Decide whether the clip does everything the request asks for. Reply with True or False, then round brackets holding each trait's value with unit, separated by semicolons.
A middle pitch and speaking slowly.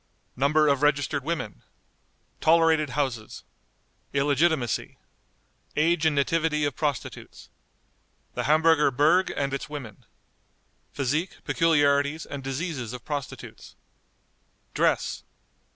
True (145 Hz; 95 wpm)